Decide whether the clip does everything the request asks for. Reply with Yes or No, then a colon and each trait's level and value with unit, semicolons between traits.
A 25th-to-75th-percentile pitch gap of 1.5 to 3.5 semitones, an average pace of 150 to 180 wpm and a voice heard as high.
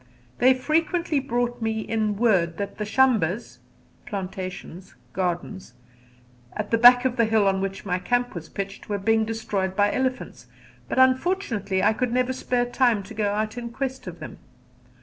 No: average, 4.1 semitones; average, 170 wpm; high, 220 Hz